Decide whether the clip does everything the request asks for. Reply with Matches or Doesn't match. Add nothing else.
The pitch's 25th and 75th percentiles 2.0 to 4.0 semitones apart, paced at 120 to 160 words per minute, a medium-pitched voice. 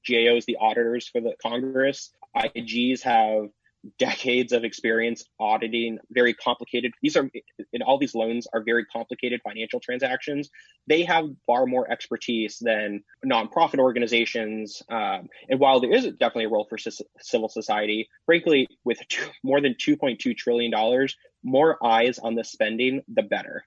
Doesn't match